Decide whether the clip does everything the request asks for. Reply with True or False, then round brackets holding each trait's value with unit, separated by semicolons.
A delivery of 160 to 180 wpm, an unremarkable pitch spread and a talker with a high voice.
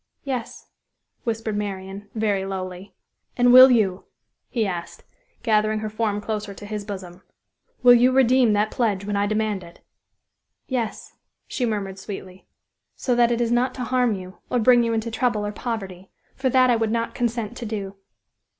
True (170 wpm; 3.2 semitones; 215 Hz)